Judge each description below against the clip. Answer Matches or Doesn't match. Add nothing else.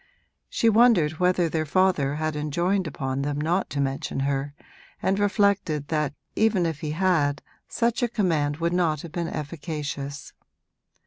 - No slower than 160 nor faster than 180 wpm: Doesn't match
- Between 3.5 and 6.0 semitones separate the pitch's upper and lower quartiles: Matches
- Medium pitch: Matches